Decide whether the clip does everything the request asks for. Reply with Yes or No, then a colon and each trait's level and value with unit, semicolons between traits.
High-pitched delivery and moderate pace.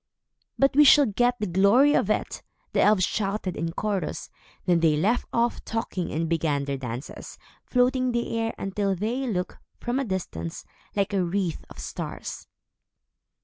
Yes: high, 200 Hz; average, 165 wpm